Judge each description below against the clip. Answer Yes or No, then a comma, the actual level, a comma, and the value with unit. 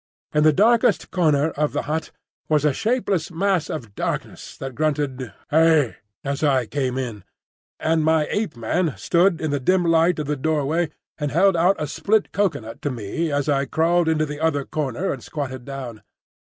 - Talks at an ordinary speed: Yes, average, 185 wpm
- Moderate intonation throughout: Yes, average, 3.3 semitones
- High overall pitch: No, medium, 155 Hz